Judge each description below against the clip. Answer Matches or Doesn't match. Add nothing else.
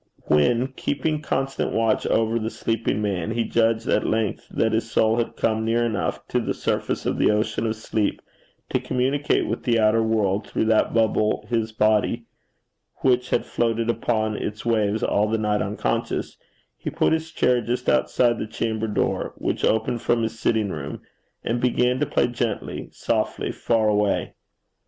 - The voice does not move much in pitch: Matches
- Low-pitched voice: Matches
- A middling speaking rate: Matches